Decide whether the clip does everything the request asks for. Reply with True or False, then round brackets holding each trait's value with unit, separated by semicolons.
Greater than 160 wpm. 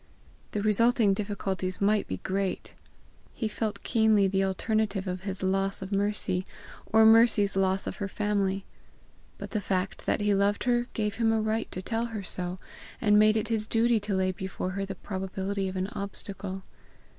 True (180 wpm)